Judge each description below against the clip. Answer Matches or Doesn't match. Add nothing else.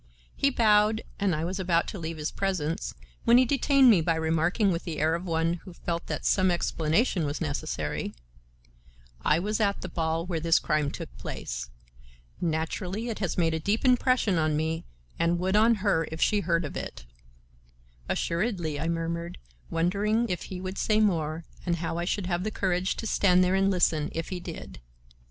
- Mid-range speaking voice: Matches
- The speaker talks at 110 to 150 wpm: Doesn't match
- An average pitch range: Matches